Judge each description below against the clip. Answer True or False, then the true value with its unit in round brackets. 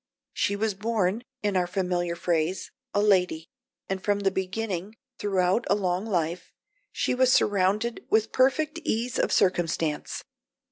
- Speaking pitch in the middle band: False (195 Hz)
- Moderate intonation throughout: True (3.4 semitones)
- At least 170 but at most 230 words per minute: False (140 wpm)